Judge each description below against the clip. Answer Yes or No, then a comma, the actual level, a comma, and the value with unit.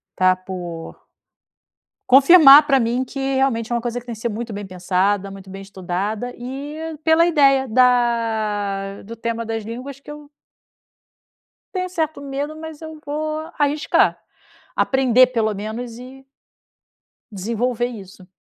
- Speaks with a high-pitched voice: Yes, high, 240 Hz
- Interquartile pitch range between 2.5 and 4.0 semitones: No, average, 5.2 semitones